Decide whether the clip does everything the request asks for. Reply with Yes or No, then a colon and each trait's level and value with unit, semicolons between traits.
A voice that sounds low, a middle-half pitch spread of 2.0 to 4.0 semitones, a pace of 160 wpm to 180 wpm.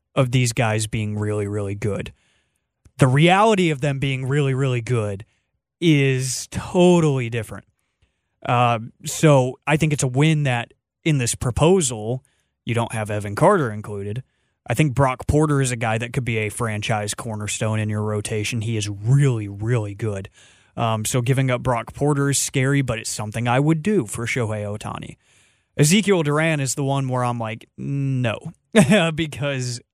No: low, 125 Hz; average, 4.6 semitones; average, 165 wpm